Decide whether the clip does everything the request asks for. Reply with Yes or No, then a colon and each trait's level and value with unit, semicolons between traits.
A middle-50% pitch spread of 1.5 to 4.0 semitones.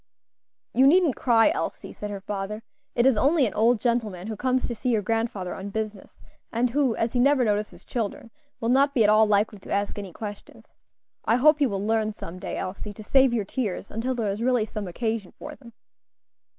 Yes: average, 3.4 semitones